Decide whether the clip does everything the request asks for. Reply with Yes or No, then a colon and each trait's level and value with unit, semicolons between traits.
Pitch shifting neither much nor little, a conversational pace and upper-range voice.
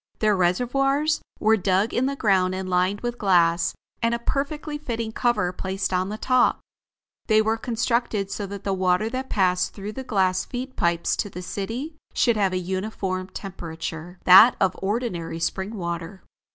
Yes: average, 4.3 semitones; average, 170 wpm; high, 200 Hz